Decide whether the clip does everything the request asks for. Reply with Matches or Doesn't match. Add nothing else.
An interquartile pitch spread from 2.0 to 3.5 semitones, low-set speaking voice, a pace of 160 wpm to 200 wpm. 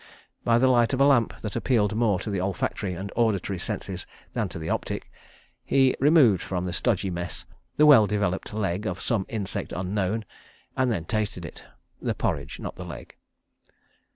Doesn't match